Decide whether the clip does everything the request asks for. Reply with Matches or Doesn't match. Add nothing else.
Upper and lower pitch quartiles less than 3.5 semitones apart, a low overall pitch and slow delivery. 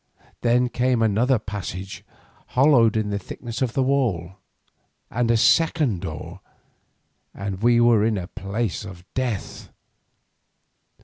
Doesn't match